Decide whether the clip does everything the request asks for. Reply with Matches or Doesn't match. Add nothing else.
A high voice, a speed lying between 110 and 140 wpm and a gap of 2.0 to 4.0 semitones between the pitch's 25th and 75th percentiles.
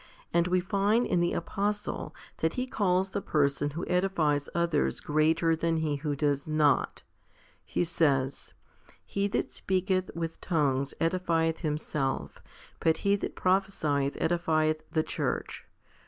Doesn't match